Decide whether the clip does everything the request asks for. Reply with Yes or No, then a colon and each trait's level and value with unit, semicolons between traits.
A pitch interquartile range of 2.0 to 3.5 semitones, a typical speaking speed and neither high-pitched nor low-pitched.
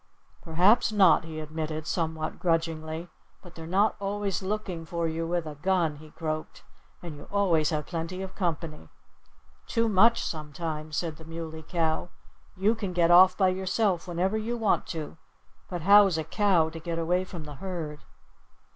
Yes: average, 3.0 semitones; average, 165 wpm; medium, 170 Hz